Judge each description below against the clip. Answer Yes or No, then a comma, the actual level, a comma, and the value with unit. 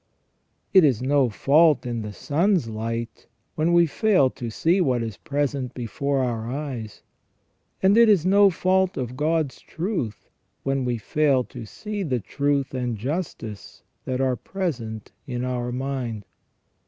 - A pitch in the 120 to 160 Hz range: Yes, low, 135 Hz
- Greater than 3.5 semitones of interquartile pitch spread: Yes, average, 5.3 semitones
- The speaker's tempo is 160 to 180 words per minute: No, average, 150 wpm